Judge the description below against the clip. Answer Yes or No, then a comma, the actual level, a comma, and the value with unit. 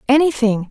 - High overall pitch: Yes, very high, 250 Hz